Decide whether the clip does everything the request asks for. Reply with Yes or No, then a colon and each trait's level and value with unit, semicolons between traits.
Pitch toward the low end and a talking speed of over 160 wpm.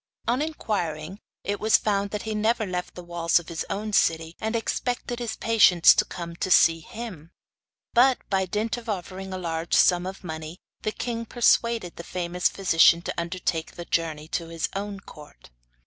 No: medium, 185 Hz; average, 180 wpm